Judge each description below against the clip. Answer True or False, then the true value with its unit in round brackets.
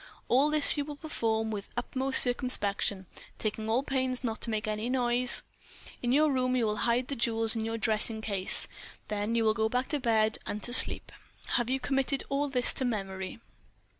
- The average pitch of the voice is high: True (235 Hz)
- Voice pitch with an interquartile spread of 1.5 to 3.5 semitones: True (3.0 semitones)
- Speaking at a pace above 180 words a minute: True (195 wpm)